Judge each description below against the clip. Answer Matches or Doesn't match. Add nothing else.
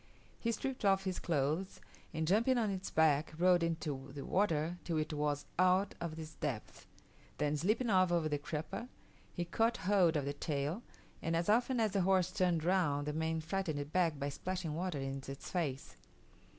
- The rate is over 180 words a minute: Matches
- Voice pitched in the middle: Matches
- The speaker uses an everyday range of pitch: Matches